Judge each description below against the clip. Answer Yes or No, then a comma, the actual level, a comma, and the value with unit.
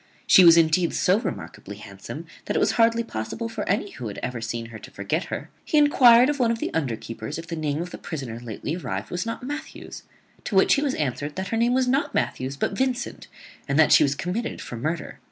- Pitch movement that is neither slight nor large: No, wide, 9.0 semitones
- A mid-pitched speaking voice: Yes, medium, 175 Hz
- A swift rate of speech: Yes, fast, 230 wpm